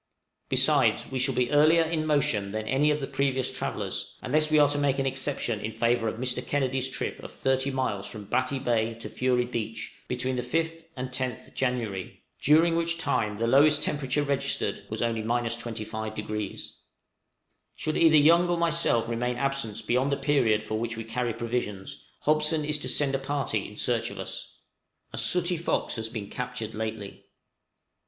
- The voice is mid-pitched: No, low, 130 Hz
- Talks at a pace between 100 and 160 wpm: No, average, 175 wpm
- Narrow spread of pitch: No, average, 4.3 semitones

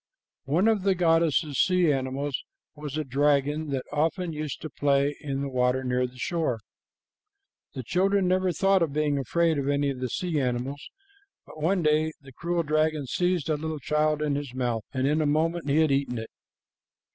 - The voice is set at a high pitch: No, medium, 150 Hz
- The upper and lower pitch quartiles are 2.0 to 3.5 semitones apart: Yes, average, 3.2 semitones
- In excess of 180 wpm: Yes, average, 190 wpm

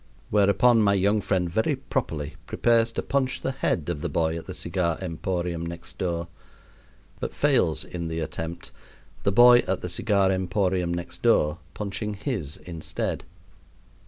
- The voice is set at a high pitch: No, very low, 95 Hz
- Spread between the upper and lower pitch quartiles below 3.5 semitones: No, average, 3.8 semitones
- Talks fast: No, average, 155 wpm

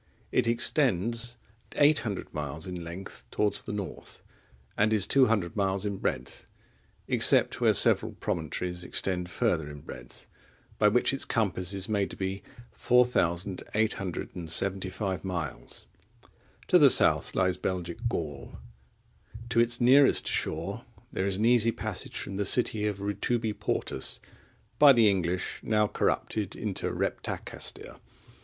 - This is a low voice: Yes, low, 100 Hz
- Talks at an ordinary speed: No, slow, 130 wpm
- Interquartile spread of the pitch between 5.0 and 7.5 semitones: No, average, 4.0 semitones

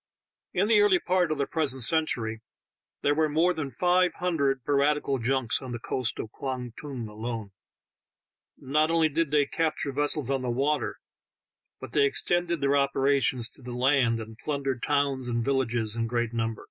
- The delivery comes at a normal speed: Yes, average, 170 wpm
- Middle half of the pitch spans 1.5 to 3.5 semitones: No, average, 4.0 semitones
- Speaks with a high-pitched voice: No, medium, 140 Hz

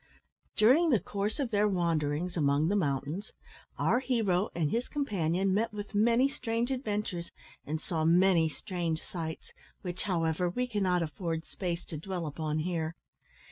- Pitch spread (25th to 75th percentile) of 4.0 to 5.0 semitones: Yes, average, 4.6 semitones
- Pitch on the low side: No, medium, 180 Hz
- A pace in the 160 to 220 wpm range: No, average, 150 wpm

